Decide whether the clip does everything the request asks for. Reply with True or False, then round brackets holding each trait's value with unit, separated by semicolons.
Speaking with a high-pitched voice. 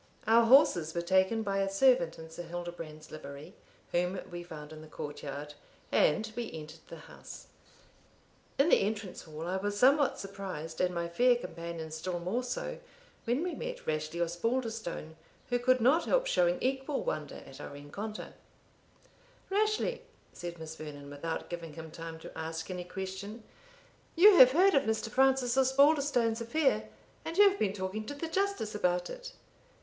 True (195 Hz)